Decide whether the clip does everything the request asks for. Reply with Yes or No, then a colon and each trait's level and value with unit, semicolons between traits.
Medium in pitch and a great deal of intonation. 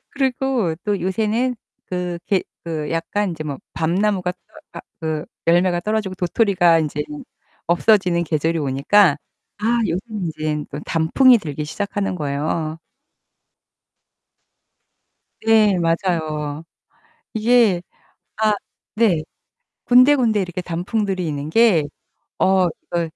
No: medium, 180 Hz; average, 4.8 semitones